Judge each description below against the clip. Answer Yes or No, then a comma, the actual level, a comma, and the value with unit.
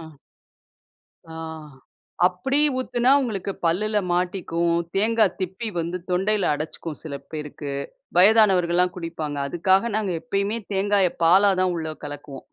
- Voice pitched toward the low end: No, medium, 185 Hz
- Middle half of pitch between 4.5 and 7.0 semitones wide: No, average, 3.7 semitones